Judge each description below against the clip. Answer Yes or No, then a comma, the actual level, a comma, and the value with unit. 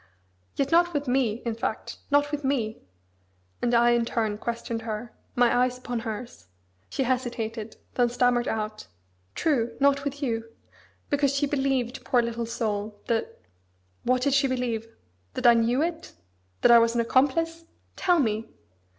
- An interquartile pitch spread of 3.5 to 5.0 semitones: No, average, 3.1 semitones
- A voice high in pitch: Yes, high, 245 Hz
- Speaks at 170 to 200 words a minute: No, average, 160 wpm